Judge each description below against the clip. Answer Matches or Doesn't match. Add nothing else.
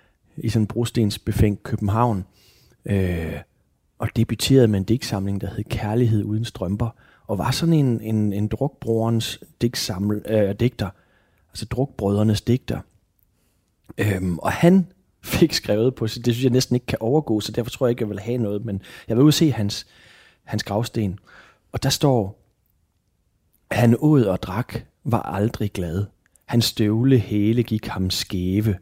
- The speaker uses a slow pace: Doesn't match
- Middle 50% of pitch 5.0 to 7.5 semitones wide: Doesn't match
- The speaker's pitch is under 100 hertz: Doesn't match